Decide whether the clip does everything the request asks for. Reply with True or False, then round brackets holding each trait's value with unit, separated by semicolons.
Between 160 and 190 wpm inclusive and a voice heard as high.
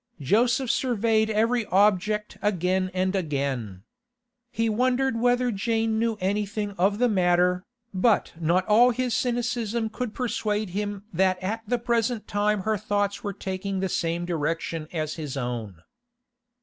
False (140 wpm; 205 Hz)